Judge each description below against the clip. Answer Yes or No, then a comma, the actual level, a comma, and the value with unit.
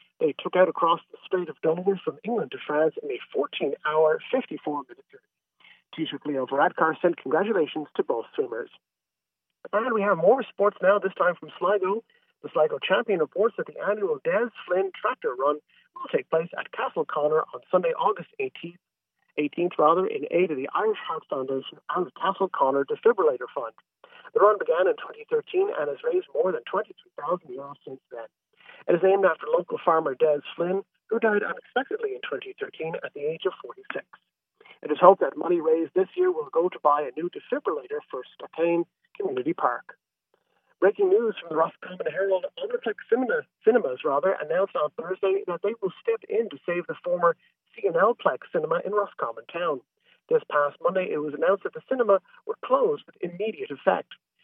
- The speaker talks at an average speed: Yes, average, 185 wpm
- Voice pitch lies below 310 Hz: No, very high, 375 Hz